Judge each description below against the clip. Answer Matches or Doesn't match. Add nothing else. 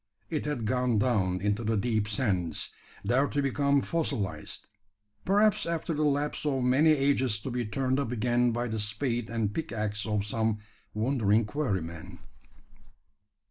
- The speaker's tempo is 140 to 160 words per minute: Matches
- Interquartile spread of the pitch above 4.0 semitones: Matches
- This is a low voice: Matches